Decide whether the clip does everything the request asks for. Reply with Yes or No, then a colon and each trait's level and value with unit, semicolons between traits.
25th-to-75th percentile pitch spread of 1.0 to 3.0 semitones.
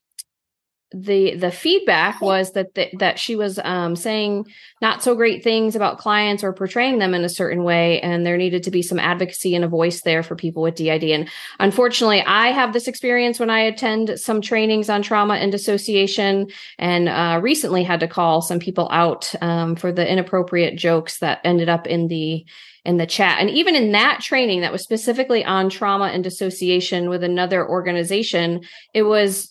No: average, 3.6 semitones